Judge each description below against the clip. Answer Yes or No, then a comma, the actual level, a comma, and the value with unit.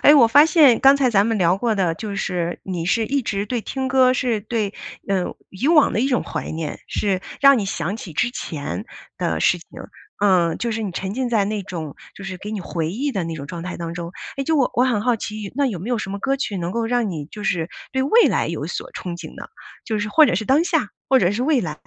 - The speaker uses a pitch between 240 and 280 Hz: No, high, 210 Hz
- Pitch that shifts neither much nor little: No, wide, 5.9 semitones